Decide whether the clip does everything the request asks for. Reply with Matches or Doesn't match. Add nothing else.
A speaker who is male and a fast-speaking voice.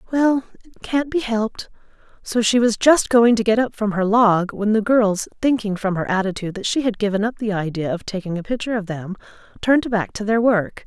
Doesn't match